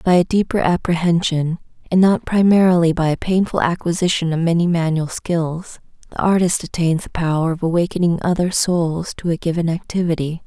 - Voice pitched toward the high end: No, medium, 170 Hz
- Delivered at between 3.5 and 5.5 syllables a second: Yes, 5.4 syllables/s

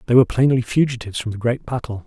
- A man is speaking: Yes, male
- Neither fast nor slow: No, fast, 235 wpm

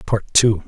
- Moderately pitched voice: No, low, 105 Hz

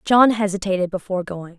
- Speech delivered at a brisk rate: No, average, 150 wpm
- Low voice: No, high, 195 Hz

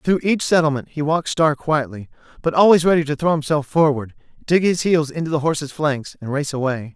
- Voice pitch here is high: No, medium, 150 Hz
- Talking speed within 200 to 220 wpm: Yes, fast, 205 wpm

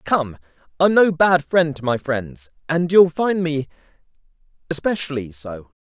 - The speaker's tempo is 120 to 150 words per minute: Yes, slow, 135 wpm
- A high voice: No, medium, 150 Hz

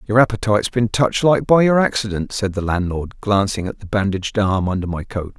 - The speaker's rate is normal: No, fast, 210 wpm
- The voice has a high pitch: No, low, 105 Hz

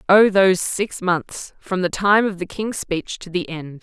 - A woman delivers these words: Yes, female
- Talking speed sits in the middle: No, fast, 220 wpm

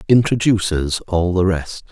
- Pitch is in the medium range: No, very low, 95 Hz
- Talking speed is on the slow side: Yes, slow, 125 wpm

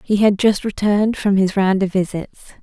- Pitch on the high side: Yes, high, 200 Hz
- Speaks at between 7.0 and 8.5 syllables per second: No, 5.4 syllables/s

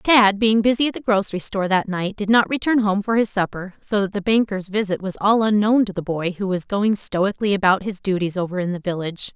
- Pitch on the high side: Yes, high, 200 Hz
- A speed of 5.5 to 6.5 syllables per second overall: Yes, 5.8 syllables/s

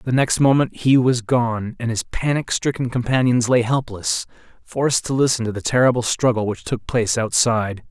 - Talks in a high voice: No, low, 120 Hz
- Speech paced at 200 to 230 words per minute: No, average, 180 wpm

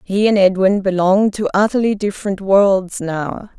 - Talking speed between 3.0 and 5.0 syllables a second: Yes, 4.8 syllables/s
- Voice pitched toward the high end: Yes, high, 195 Hz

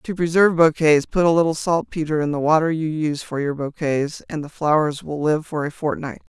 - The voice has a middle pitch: Yes, medium, 155 Hz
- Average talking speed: No, fast, 215 wpm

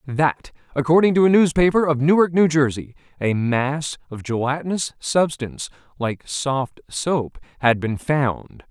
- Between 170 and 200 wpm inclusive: No, average, 140 wpm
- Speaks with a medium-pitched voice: Yes, medium, 145 Hz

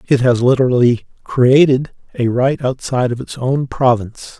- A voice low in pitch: Yes, low, 125 Hz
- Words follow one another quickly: No, average, 150 wpm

